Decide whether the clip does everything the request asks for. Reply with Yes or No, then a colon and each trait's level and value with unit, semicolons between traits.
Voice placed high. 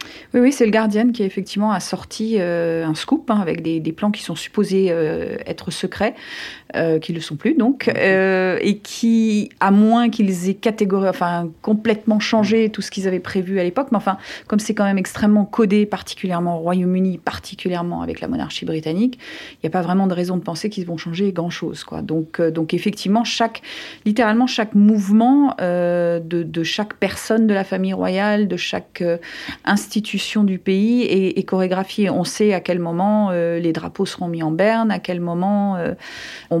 Yes: high, 195 Hz